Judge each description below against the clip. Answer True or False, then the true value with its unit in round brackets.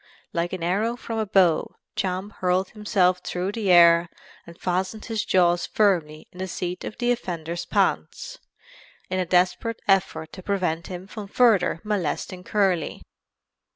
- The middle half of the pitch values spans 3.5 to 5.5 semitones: False (2.8 semitones)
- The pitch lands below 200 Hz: True (185 Hz)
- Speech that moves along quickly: False (155 wpm)